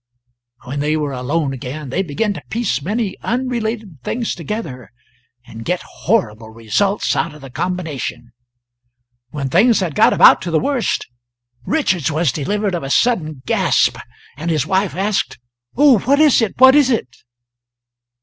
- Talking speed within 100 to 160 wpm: Yes, average, 155 wpm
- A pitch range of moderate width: No, wide, 7.9 semitones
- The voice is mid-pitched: Yes, medium, 175 Hz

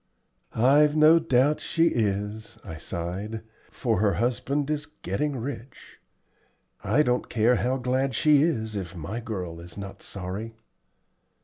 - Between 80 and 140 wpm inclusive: Yes, slow, 135 wpm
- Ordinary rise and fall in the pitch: No, wide, 5.9 semitones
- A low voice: Yes, low, 115 Hz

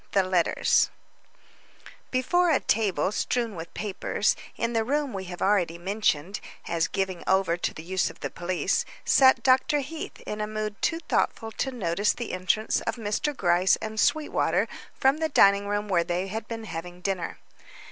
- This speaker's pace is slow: No, average, 170 wpm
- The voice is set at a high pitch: Yes, high, 205 Hz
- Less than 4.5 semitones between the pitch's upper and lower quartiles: No, average, 4.9 semitones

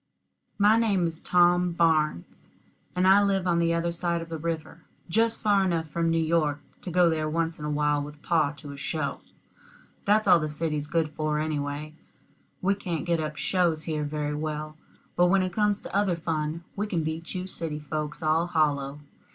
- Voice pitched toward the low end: No, medium, 165 Hz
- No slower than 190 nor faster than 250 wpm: Yes, average, 195 wpm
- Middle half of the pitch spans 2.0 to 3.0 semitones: Yes, average, 2.7 semitones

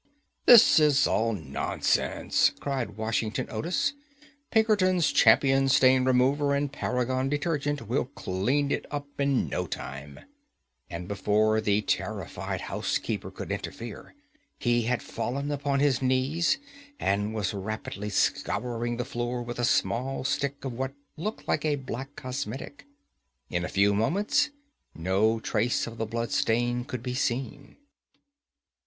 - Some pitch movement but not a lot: Yes, average, 4.2 semitones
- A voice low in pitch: Yes, low, 125 Hz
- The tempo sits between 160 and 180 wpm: No, slow, 135 wpm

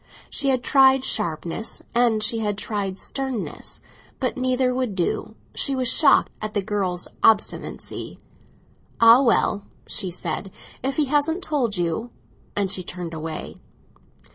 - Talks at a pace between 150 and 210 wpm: No, average, 140 wpm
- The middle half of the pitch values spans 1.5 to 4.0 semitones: No, average, 5.2 semitones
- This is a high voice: Yes, high, 225 Hz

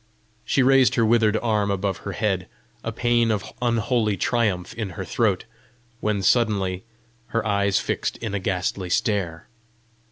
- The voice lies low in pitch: Yes, low, 105 Hz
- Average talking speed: Yes, average, 150 wpm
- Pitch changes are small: No, average, 3.2 semitones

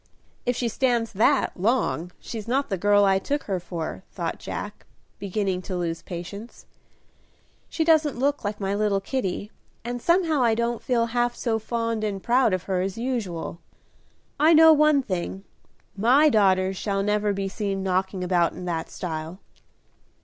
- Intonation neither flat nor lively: Yes, average, 4.4 semitones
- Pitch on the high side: Yes, high, 210 Hz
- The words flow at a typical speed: Yes, average, 165 wpm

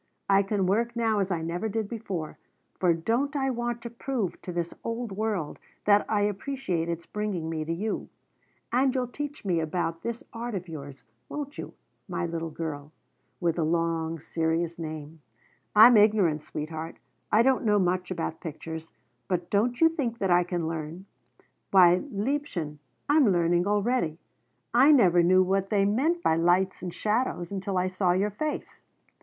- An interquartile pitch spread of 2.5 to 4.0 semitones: No, wide, 5.4 semitones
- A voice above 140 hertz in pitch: Yes, high, 190 Hz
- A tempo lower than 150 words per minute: No, average, 170 wpm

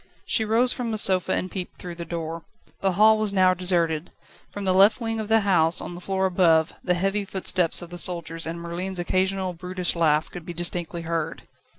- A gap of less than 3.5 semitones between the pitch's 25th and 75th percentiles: Yes, narrow, 2.4 semitones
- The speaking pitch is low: No, medium, 180 Hz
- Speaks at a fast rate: Yes, fast, 210 wpm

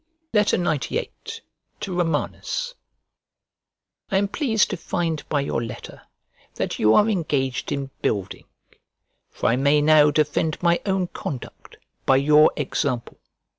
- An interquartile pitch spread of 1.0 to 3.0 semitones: No, average, 4.6 semitones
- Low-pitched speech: No, medium, 150 Hz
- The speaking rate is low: Yes, slow, 125 wpm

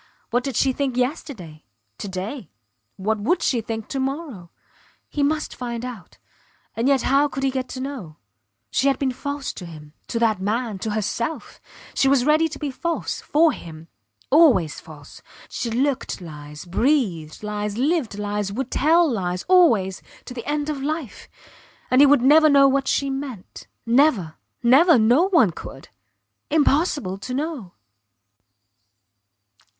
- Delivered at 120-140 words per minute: No, average, 155 wpm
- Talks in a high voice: Yes, very high, 255 Hz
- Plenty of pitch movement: Yes, wide, 5.8 semitones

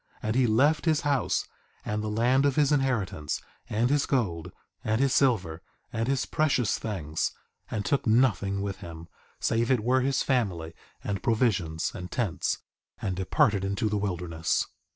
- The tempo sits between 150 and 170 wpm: Yes, average, 160 wpm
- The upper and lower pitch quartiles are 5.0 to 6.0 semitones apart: Yes, wide, 5.6 semitones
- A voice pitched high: No, low, 110 Hz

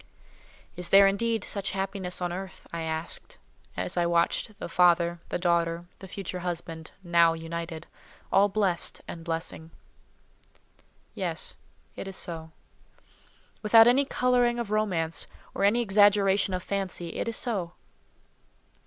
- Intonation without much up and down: No, average, 3.2 semitones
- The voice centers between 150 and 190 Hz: Yes, medium, 185 Hz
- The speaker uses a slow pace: Yes, slow, 130 wpm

